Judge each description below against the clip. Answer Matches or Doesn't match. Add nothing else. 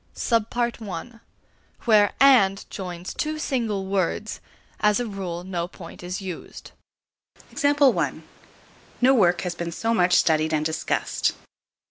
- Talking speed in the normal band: Doesn't match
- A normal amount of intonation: Matches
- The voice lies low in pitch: Doesn't match